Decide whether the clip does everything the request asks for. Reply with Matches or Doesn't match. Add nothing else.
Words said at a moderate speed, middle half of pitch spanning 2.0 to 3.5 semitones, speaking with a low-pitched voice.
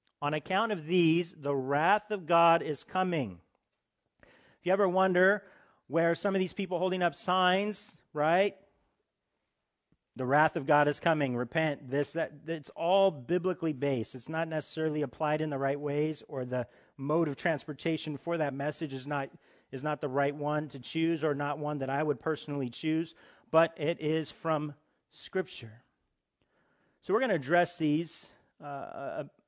Doesn't match